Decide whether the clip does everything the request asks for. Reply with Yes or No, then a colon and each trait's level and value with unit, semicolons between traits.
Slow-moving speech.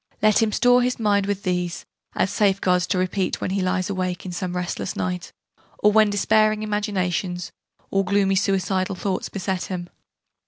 No: average, 165 wpm